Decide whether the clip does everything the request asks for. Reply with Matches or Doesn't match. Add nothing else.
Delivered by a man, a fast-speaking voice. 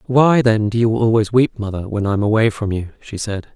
Matches